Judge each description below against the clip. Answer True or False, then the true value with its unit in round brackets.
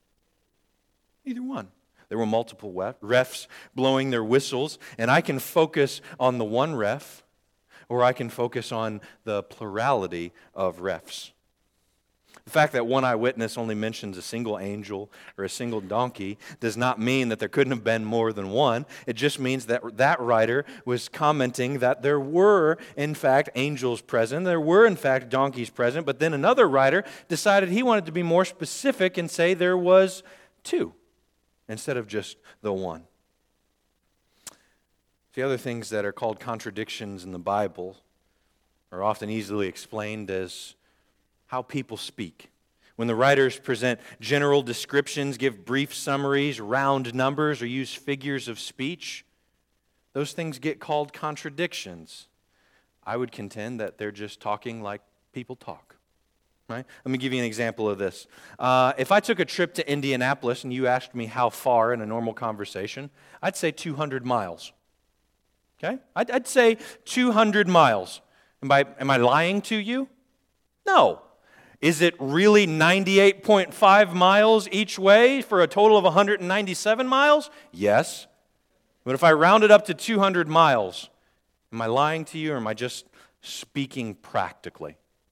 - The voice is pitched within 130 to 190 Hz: True (135 Hz)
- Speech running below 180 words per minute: True (155 wpm)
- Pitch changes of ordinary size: False (6.7 semitones)